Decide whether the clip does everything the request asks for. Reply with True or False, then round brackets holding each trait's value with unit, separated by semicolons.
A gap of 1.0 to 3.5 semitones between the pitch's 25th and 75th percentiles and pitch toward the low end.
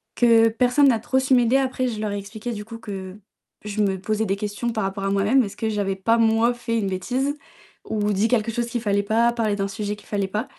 False (2.8 semitones; 220 Hz)